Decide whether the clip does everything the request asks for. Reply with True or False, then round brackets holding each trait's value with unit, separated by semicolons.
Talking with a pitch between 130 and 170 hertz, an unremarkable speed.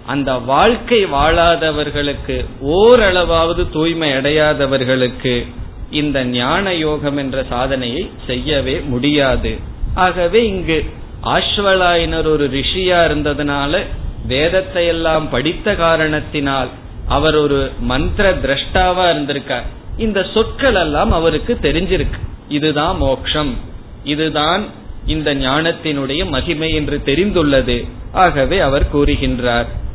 True (150 Hz; 90 wpm)